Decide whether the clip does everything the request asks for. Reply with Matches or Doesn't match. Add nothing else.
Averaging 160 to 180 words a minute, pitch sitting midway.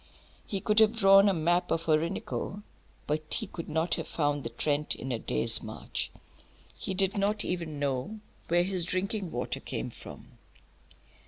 Matches